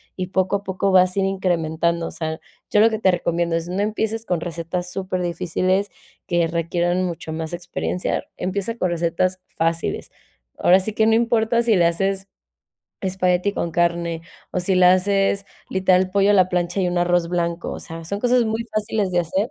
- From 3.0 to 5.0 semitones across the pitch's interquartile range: No, narrow, 2.4 semitones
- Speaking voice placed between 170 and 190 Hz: Yes, medium, 185 Hz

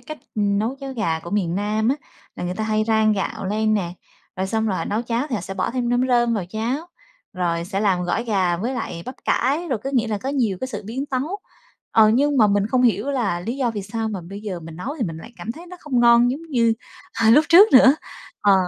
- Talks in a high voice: Yes, high, 220 Hz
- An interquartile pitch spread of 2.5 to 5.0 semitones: Yes, average, 4.3 semitones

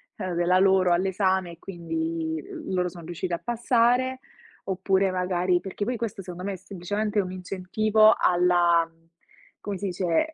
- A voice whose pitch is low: No, medium, 185 Hz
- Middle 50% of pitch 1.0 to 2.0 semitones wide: No, narrow, 2.5 semitones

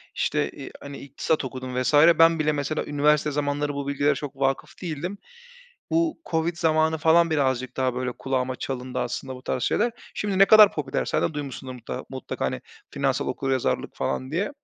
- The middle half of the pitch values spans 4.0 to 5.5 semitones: No, average, 3.5 semitones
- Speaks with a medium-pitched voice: Yes, medium, 145 Hz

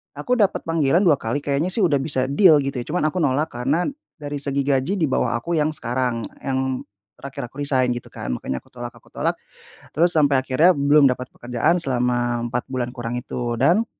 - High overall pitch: No, medium, 140 Hz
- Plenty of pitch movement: No, average, 3.9 semitones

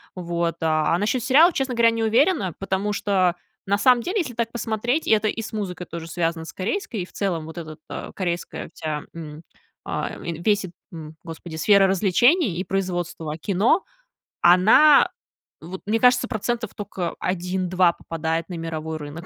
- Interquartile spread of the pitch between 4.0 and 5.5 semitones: Yes, average, 5.0 semitones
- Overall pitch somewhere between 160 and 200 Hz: Yes, medium, 185 Hz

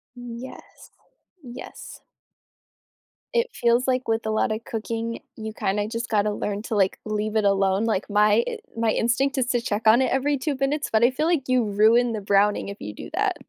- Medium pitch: No, high, 225 Hz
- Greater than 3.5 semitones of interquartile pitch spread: No, average, 3.0 semitones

